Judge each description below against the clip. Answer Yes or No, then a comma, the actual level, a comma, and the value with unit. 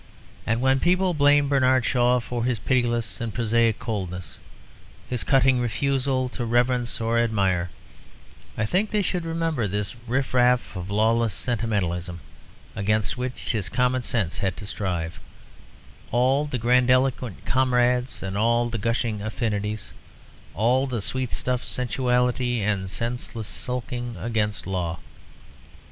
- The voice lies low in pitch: Yes, low, 120 Hz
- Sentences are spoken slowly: Yes, slow, 125 wpm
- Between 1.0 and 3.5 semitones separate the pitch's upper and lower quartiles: Yes, average, 3.1 semitones